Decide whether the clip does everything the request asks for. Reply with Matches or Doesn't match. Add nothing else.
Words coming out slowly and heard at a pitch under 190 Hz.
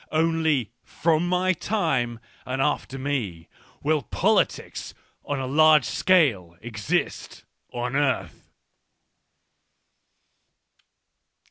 Matches